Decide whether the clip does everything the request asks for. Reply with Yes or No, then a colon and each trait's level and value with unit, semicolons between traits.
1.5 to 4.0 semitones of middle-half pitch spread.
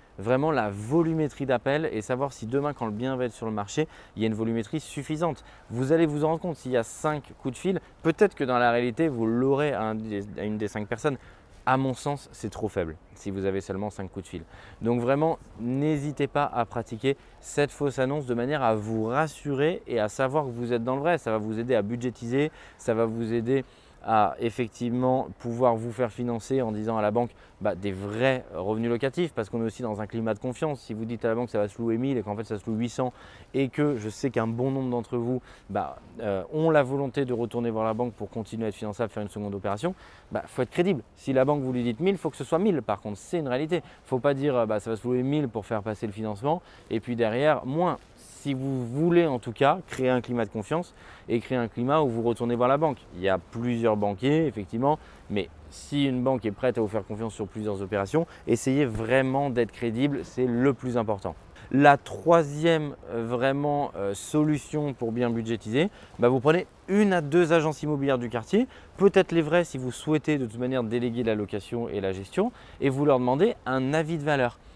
No: average, 4.5 semitones